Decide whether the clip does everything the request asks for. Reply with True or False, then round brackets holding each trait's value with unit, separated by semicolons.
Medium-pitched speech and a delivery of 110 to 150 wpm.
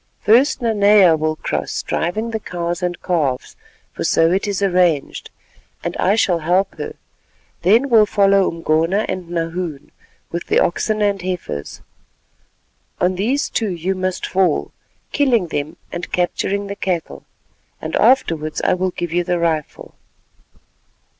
True (180 Hz; 140 wpm)